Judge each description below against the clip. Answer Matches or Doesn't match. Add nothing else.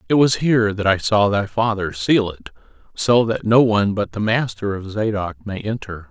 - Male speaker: Matches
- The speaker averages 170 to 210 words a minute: Matches